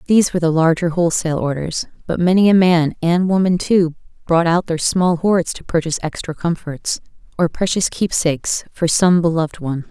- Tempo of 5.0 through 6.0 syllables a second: Yes, 5.5 syllables/s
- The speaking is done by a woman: Yes, female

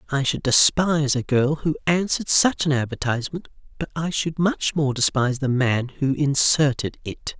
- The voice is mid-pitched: Yes, medium, 145 Hz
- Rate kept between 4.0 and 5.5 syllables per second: Yes, 5.0 syllables/s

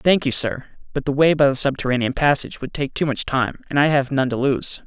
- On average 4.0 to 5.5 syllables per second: No, 5.9 syllables/s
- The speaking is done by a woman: No, male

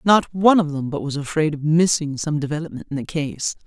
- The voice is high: No, medium, 155 Hz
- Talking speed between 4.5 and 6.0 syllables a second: Yes, 5.8 syllables/s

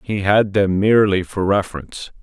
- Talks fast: No, average, 160 wpm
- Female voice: No, male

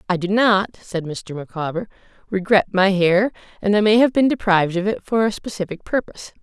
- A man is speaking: No, female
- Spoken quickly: No, average, 195 wpm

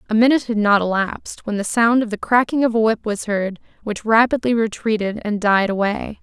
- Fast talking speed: Yes, fast, 210 wpm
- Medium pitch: No, high, 220 Hz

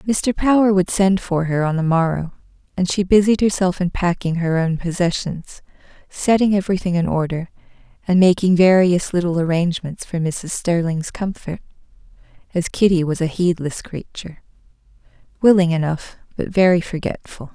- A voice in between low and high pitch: Yes, medium, 180 Hz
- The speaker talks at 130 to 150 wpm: Yes, average, 145 wpm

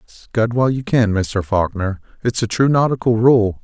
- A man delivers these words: Yes, male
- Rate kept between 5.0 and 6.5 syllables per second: No, 4.6 syllables/s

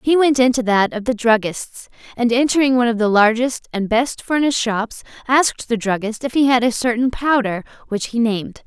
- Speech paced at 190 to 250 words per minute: Yes, average, 200 wpm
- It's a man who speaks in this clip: No, female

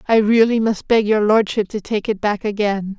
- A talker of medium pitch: No, high, 210 Hz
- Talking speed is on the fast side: Yes, fast, 220 wpm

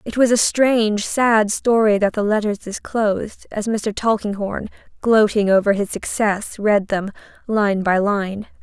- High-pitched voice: Yes, high, 210 Hz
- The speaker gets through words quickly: No, average, 155 wpm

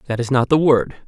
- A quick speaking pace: Yes, fast, 280 wpm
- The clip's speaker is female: No, male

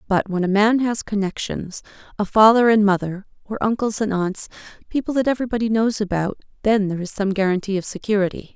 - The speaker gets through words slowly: No, average, 180 wpm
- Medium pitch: No, high, 205 Hz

